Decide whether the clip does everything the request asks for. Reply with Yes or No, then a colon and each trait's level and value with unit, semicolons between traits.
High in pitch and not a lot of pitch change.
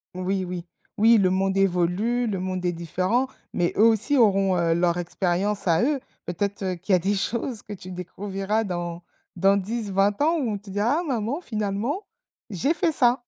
No: high, 195 Hz; average, 3.9 semitones